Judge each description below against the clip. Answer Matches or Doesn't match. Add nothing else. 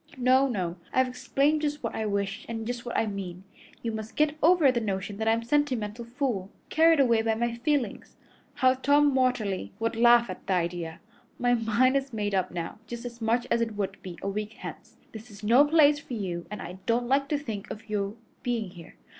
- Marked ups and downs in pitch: Doesn't match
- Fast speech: Matches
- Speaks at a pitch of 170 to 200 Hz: Doesn't match